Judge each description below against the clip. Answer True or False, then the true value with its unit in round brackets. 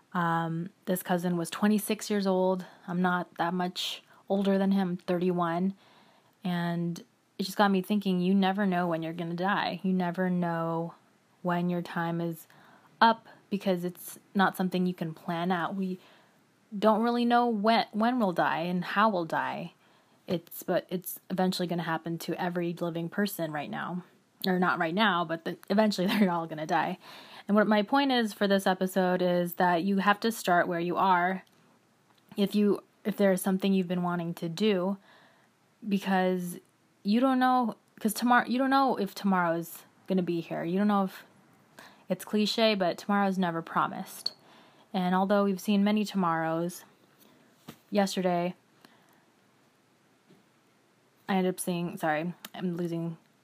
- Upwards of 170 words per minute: False (165 wpm)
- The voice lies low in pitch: False (185 Hz)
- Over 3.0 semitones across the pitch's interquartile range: False (2.7 semitones)